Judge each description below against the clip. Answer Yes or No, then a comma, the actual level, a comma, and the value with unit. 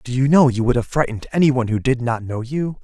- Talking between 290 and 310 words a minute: Yes, fast, 295 wpm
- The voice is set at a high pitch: No, low, 130 Hz